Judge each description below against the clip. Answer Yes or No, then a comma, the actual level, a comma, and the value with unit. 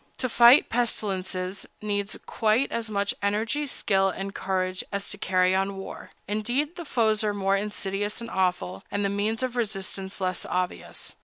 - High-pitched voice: Yes, high, 200 Hz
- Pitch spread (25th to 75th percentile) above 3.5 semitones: No, narrow, 2.6 semitones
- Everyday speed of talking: Yes, average, 165 wpm